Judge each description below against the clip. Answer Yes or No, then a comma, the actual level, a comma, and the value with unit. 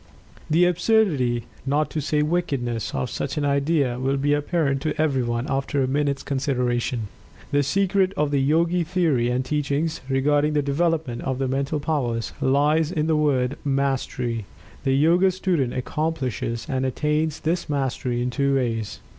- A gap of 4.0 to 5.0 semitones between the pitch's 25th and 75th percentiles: No, average, 3.1 semitones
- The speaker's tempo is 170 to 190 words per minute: No, average, 155 wpm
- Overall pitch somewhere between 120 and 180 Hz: Yes, medium, 140 Hz